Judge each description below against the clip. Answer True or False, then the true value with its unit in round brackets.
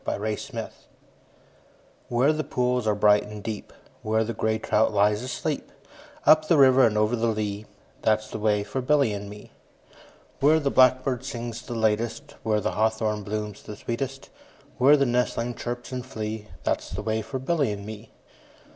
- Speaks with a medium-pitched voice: False (110 Hz)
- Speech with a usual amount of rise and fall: True (3.2 semitones)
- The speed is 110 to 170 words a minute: False (185 wpm)